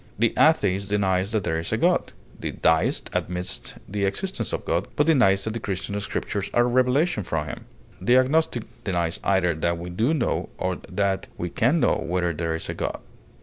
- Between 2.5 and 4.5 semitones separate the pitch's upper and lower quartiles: No, average, 5.3 semitones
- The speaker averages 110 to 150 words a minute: No, average, 195 wpm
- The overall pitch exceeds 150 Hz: No, low, 100 Hz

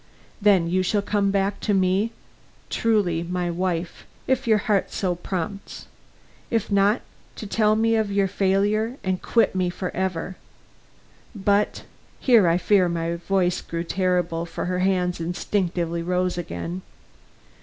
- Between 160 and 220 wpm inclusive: No, average, 145 wpm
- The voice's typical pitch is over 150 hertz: Yes, medium, 185 Hz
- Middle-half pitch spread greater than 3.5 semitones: No, narrow, 2.6 semitones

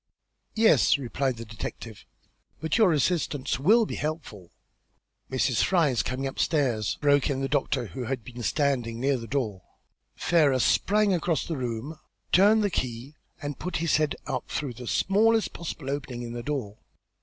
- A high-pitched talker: No, medium, 140 Hz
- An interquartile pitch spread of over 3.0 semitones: Yes, average, 5.1 semitones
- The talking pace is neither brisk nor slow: Yes, average, 165 wpm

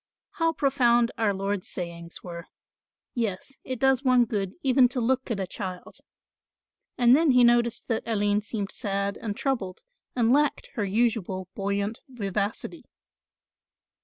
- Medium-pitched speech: No, high, 225 Hz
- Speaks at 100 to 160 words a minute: Yes, average, 140 wpm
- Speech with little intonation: No, average, 4.0 semitones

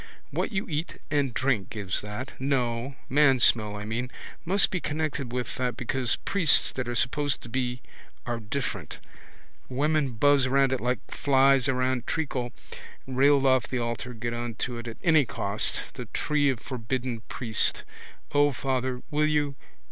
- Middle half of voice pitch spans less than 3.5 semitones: Yes, average, 2.9 semitones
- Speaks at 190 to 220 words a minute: No, average, 160 wpm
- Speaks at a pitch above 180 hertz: No, low, 130 Hz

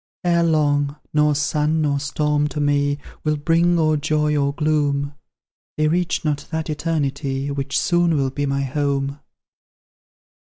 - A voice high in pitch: No, medium, 150 Hz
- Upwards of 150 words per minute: No, average, 145 wpm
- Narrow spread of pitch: Yes, narrow, 1.6 semitones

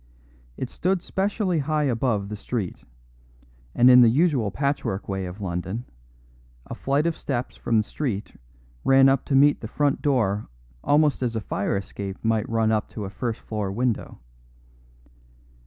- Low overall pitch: Yes, low, 120 Hz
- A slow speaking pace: No, average, 160 wpm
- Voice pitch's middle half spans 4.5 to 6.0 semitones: Yes, average, 5.1 semitones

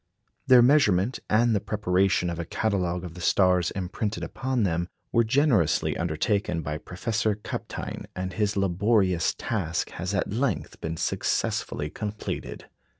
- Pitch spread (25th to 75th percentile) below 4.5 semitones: Yes, average, 3.8 semitones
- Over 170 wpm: No, average, 140 wpm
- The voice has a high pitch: No, very low, 95 Hz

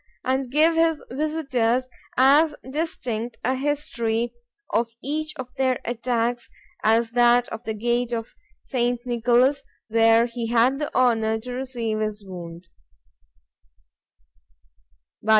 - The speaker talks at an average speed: No, slow, 120 wpm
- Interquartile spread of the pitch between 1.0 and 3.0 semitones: Yes, narrow, 2.6 semitones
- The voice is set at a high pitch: Yes, high, 245 Hz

